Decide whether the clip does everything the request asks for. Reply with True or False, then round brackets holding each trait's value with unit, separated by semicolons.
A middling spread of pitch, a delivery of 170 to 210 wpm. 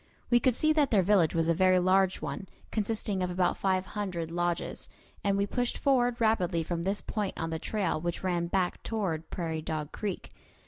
True (3.5 semitones; 195 wpm)